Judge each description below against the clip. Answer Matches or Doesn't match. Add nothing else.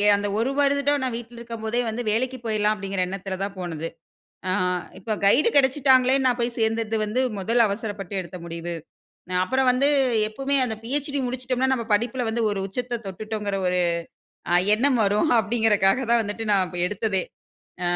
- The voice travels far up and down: Doesn't match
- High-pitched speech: Matches